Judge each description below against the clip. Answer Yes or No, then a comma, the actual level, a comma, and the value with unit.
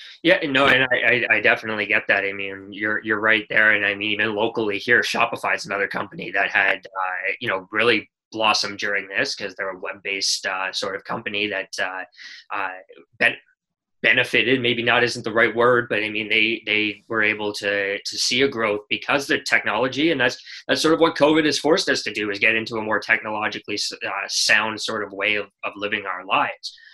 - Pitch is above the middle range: No, low, 110 Hz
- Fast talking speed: Yes, fast, 210 wpm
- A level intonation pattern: Yes, narrow, 1.7 semitones